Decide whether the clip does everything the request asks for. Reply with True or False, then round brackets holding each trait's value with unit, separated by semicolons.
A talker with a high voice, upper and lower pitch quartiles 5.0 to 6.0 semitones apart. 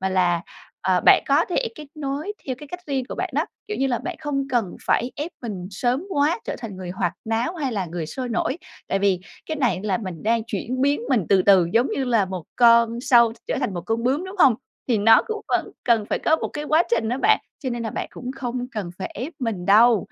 True (240 Hz; 5.5 semitones)